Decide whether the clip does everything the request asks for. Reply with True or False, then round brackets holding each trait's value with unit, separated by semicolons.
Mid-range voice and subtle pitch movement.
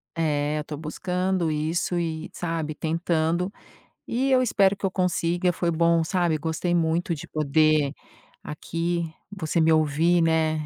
True (165 Hz; 1.9 semitones)